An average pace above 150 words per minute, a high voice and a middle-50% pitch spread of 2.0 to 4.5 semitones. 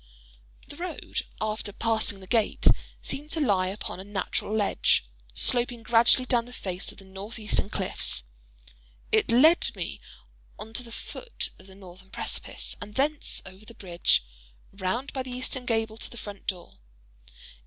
Yes: average, 165 wpm; high, 220 Hz; average, 4.2 semitones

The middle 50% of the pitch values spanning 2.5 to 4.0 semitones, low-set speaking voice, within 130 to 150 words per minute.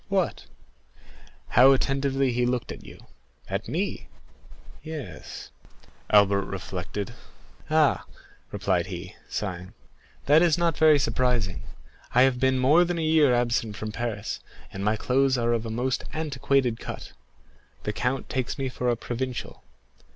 Yes: average, 3.5 semitones; low, 125 Hz; average, 140 wpm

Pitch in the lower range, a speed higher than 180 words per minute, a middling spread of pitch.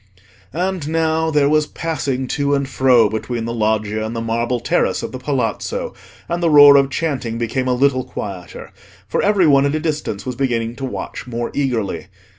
Yes: low, 130 Hz; average, 190 wpm; average, 4.1 semitones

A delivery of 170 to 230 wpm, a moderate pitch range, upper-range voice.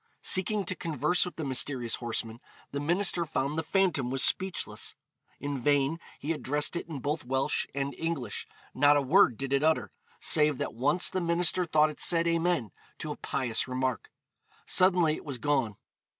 No: average, 175 wpm; average, 4.1 semitones; medium, 150 Hz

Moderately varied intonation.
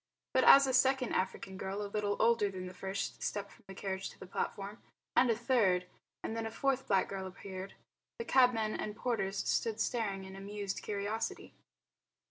Yes: average, 3.0 semitones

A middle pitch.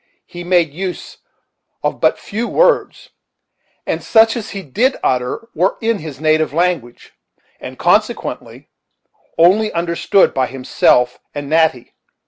Yes: medium, 170 Hz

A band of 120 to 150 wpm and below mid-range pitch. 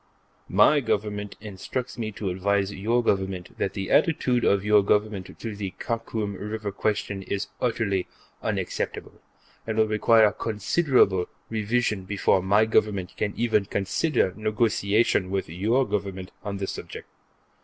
Yes: slow, 135 wpm; low, 105 Hz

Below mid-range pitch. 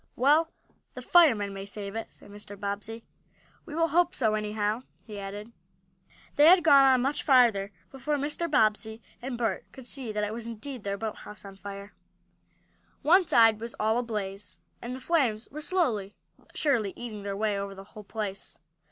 No: high, 225 Hz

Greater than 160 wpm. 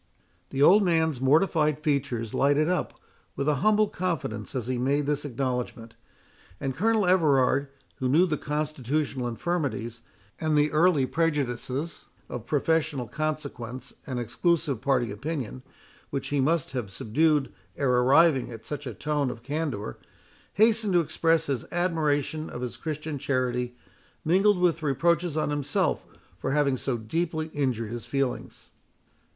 No: average, 140 wpm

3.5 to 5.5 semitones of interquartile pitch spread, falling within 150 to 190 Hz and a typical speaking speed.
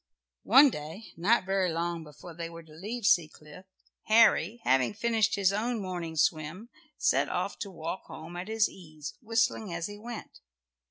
Yes: average, 5.2 semitones; medium, 185 Hz; average, 165 wpm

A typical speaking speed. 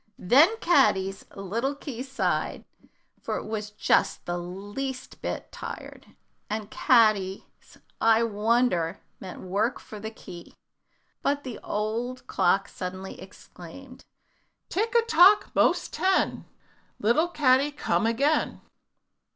No: slow, 115 wpm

